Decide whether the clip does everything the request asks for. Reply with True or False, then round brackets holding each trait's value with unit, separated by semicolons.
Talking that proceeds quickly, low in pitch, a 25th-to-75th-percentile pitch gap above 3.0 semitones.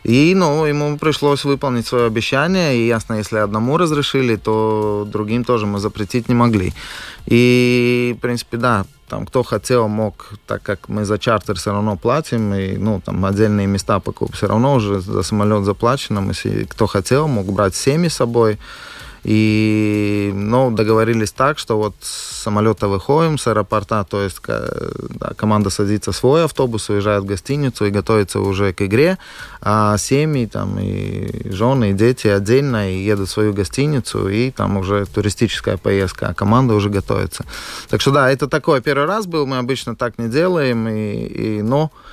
True (170 wpm; 110 Hz; 3.5 semitones)